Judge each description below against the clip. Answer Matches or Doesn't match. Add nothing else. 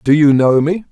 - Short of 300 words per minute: Matches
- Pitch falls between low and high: Matches